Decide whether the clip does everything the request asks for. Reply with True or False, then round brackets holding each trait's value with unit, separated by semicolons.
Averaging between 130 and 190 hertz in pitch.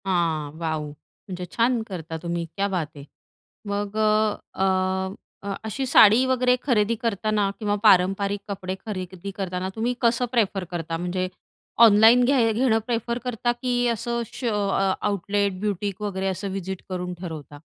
False (200 Hz)